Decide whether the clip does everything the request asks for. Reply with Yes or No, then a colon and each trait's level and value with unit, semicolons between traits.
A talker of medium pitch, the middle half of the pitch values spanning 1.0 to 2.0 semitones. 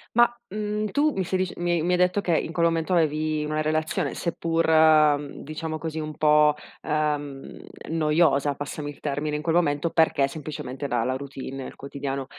No: medium, 155 Hz; narrow, 2.4 semitones